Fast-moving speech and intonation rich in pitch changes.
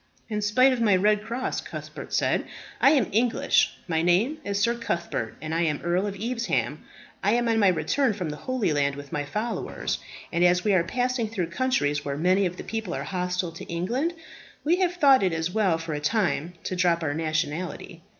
Yes: fast, 210 wpm; wide, 5.8 semitones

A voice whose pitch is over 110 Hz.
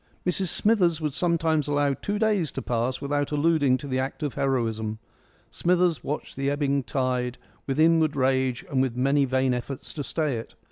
Yes: medium, 140 Hz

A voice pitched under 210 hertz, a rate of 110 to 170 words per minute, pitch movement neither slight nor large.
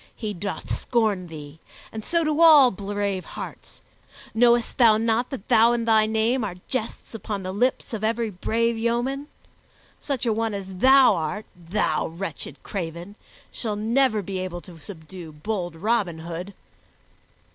No: high, 215 Hz; average, 155 wpm; average, 4.1 semitones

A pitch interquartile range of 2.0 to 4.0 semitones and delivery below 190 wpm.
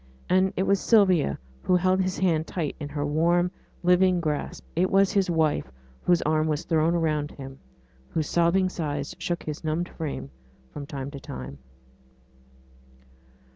Yes: average, 3.5 semitones; average, 155 wpm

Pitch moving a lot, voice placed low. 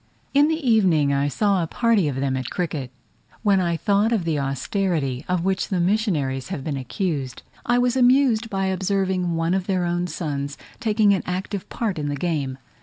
No: wide, 6.1 semitones; medium, 180 Hz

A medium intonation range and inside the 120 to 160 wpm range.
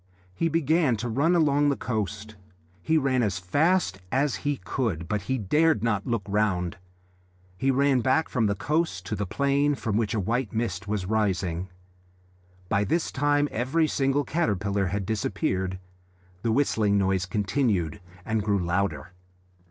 No: wide, 6.0 semitones; average, 155 wpm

